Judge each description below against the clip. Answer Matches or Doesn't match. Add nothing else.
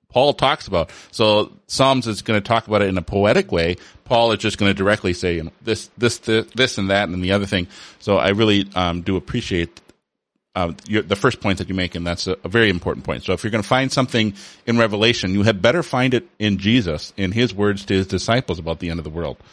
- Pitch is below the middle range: Matches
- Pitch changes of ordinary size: Matches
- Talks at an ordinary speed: Doesn't match